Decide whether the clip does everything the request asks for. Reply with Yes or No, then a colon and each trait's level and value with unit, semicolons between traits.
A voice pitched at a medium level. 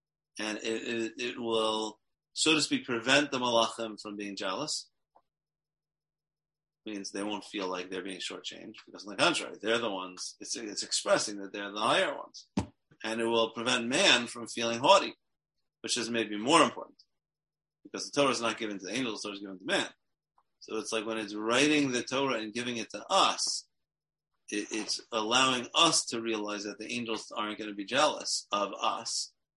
No: low, 115 Hz